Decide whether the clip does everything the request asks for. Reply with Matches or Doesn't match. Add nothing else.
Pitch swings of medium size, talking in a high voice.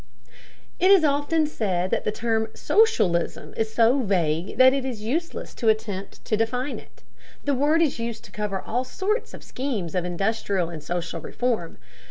Doesn't match